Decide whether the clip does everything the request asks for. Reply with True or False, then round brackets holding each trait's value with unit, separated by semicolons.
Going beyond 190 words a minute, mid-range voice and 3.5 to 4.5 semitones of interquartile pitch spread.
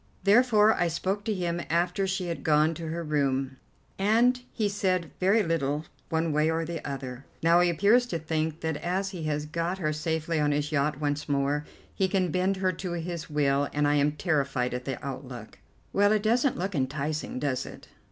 True (200 wpm; 160 Hz; 4.2 semitones)